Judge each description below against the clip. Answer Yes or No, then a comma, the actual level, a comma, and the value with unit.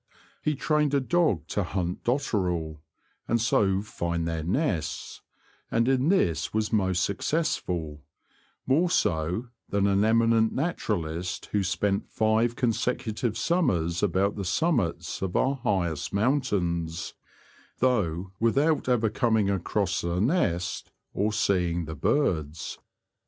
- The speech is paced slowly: Yes, slow, 125 wpm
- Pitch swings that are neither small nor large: No, wide, 6.1 semitones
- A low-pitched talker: Yes, low, 100 Hz